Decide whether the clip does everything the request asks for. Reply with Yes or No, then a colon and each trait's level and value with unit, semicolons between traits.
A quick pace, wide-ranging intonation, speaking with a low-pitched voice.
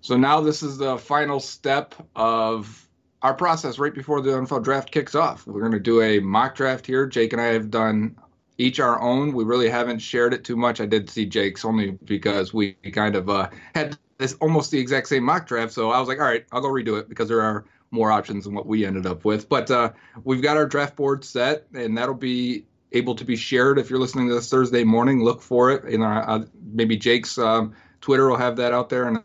No: fast, 240 wpm; average, 3.4 semitones; low, 120 Hz